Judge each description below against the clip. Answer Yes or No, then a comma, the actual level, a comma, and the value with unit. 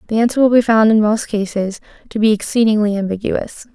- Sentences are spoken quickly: No, average, 190 wpm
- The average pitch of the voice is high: Yes, high, 215 Hz